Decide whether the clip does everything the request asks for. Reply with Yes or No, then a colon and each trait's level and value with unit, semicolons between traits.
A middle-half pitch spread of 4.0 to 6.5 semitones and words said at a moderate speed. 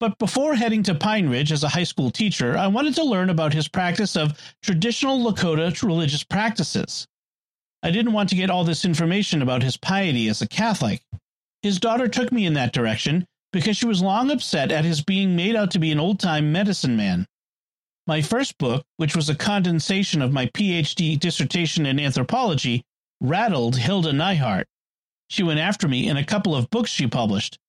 Yes: wide, 5.5 semitones; average, 190 wpm